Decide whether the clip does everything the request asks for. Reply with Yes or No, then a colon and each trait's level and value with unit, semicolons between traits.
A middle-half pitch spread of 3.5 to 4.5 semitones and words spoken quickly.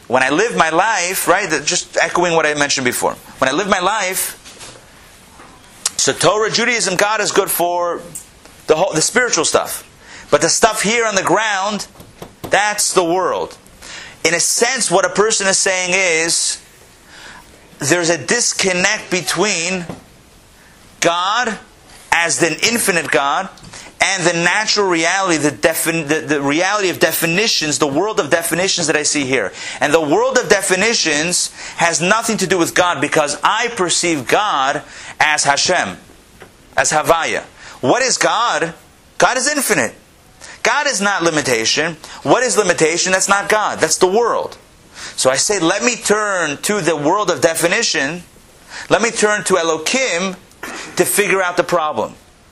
No: average, 4.1 semitones; average, 155 wpm